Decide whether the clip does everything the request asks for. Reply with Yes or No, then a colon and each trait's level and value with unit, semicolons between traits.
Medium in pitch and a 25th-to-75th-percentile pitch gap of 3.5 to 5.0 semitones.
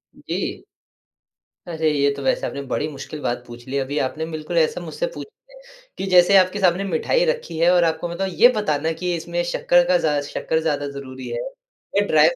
Yes: medium, 165 Hz; average, 4.2 semitones